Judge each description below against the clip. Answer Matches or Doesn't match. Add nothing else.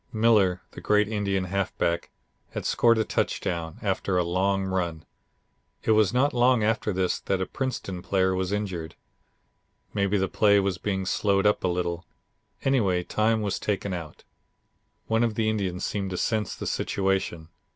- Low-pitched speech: Matches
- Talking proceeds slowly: Doesn't match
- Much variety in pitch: Doesn't match